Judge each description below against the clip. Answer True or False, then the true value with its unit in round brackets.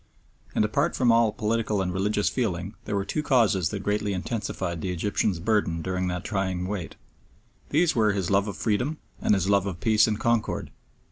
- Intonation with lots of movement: False (2.9 semitones)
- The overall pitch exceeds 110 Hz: False (105 Hz)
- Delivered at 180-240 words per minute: True (190 wpm)